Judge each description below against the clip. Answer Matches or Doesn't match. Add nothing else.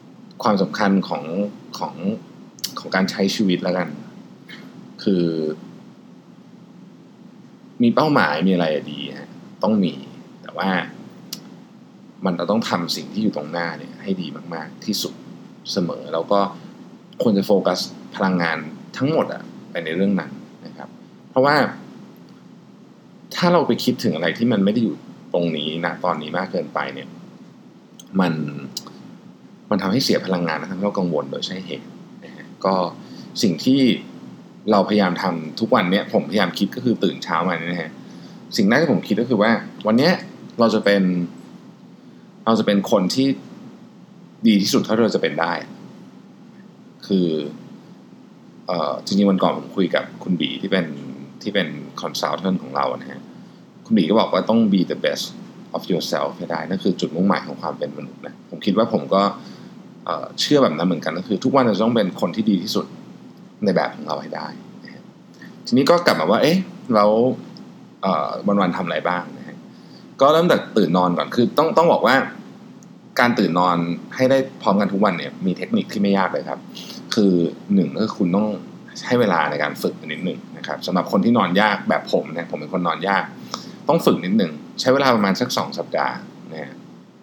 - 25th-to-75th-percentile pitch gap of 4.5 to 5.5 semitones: Doesn't match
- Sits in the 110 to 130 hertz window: Doesn't match